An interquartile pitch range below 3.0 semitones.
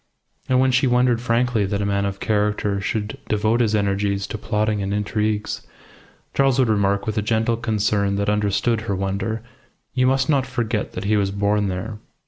Yes: narrow, 2.4 semitones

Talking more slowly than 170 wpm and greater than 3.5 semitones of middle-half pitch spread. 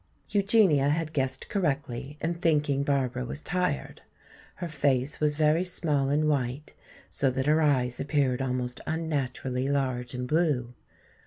No: average, 140 wpm; average, 3.2 semitones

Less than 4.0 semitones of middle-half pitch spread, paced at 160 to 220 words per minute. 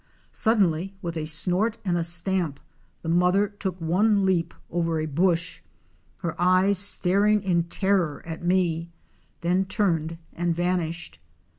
No: narrow, 2.5 semitones; slow, 135 wpm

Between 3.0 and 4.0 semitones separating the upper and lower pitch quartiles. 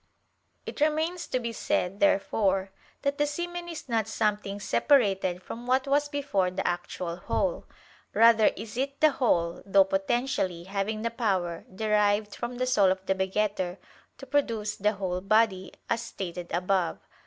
No: average, 5.0 semitones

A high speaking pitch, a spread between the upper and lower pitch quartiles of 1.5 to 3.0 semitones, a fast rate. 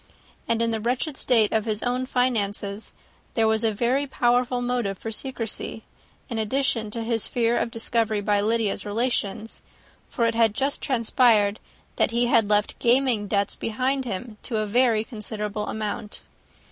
No: high, 225 Hz; narrow, 2.6 semitones; average, 160 wpm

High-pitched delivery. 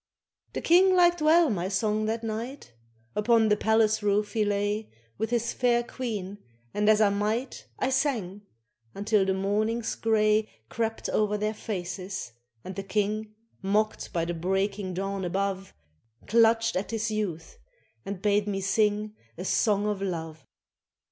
Yes: high, 210 Hz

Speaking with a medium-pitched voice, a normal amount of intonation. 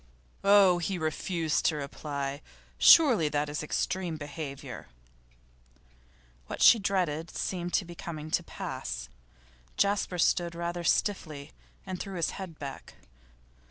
Yes: medium, 170 Hz; average, 3.8 semitones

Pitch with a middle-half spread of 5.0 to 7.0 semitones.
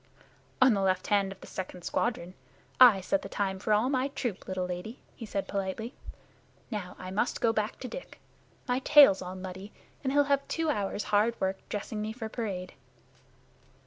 No: average, 4.5 semitones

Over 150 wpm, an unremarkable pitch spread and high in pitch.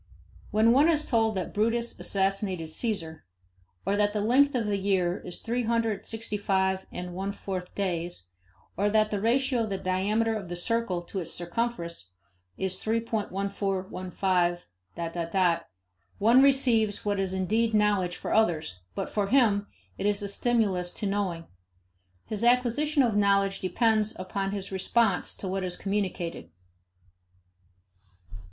No: average, 145 wpm; average, 3.4 semitones; high, 200 Hz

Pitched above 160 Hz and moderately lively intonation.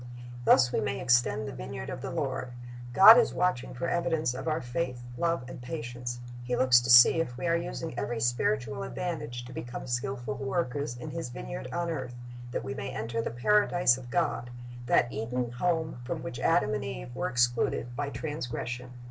No: low, 125 Hz; average, 4.4 semitones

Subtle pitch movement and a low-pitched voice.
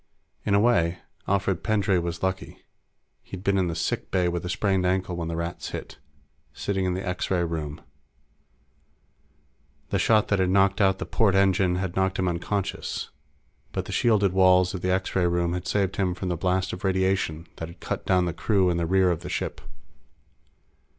Yes: narrow, 1.8 semitones; very low, 95 Hz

